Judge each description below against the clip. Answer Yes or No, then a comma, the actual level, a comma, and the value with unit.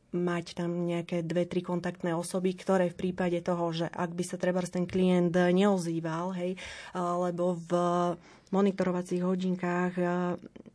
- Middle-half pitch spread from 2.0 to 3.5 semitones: No, narrow, 0.8 semitones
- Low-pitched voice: No, medium, 180 Hz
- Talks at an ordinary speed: Yes, average, 135 wpm